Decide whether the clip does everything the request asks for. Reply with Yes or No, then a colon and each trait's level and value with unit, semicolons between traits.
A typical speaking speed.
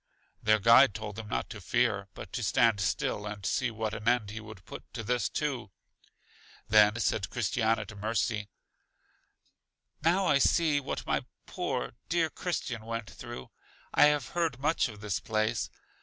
Yes: average, 165 wpm